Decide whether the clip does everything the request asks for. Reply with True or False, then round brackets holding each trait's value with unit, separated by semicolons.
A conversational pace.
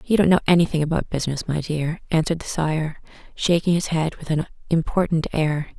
True (185 wpm)